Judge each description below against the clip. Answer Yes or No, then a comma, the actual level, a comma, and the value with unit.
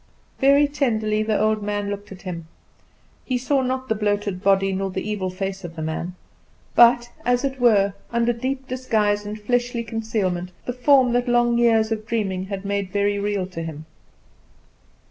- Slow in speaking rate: No, average, 175 wpm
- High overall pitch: Yes, high, 215 Hz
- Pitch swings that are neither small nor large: Yes, average, 3.7 semitones